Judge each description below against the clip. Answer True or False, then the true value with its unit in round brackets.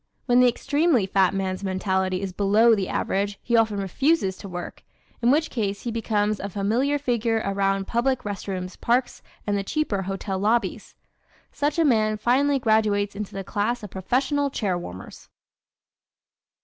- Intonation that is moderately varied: True (3.9 semitones)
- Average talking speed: True (160 wpm)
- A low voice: False (210 Hz)